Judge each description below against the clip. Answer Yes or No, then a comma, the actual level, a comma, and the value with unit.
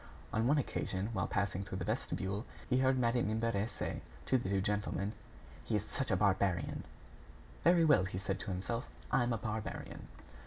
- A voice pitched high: No, low, 105 Hz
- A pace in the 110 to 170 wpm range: No, average, 185 wpm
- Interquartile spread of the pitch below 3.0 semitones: No, average, 3.5 semitones